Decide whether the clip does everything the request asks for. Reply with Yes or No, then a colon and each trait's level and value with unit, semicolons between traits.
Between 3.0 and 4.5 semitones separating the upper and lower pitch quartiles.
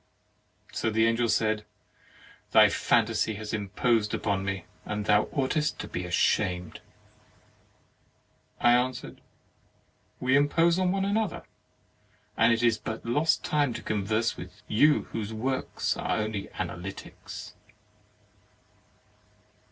Yes: average, 4.1 semitones